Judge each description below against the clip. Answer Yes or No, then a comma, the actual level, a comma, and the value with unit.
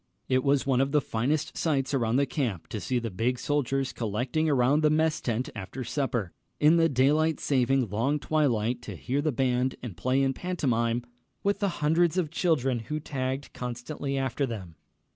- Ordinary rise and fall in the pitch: Yes, average, 3.6 semitones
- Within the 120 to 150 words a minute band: No, average, 180 wpm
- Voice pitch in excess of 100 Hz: Yes, low, 135 Hz